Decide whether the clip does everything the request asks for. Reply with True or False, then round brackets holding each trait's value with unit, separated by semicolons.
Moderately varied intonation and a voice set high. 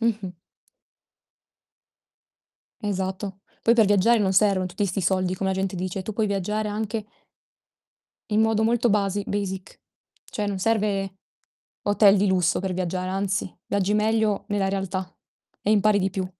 False (2.0 semitones; 200 Hz)